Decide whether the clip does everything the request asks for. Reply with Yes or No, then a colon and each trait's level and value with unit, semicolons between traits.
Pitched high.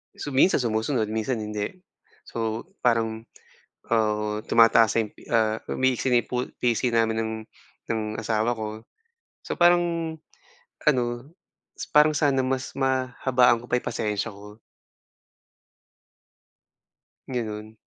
No: low, 115 Hz